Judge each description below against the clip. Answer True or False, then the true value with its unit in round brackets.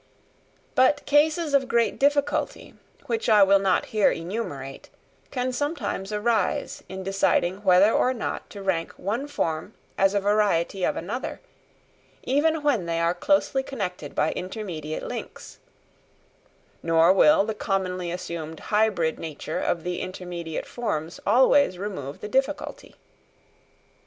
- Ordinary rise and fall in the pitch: False (6.2 semitones)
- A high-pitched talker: True (195 Hz)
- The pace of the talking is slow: True (125 wpm)